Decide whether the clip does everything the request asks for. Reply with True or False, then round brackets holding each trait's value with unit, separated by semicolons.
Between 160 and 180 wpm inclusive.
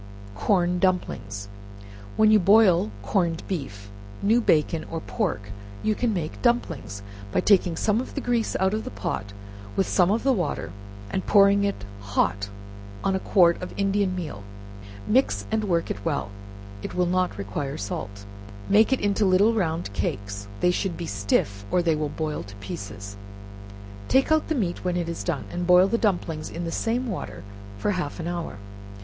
True (175 wpm)